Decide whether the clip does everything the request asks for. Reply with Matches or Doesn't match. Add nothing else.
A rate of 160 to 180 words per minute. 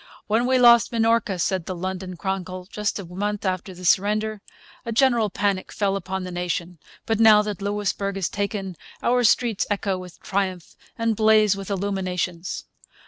Matches